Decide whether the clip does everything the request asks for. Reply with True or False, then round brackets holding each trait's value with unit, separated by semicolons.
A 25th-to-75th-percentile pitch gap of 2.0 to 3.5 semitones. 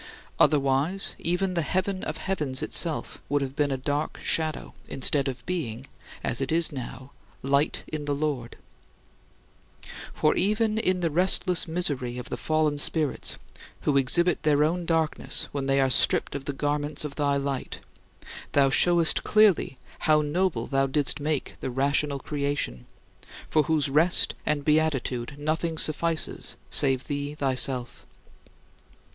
True (2.9 semitones)